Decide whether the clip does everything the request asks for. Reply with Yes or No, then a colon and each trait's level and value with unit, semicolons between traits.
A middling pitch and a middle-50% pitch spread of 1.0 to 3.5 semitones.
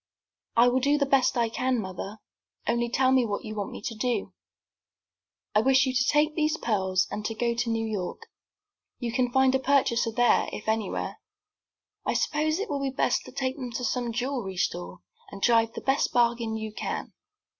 No: high, 240 Hz; average, 3.1 semitones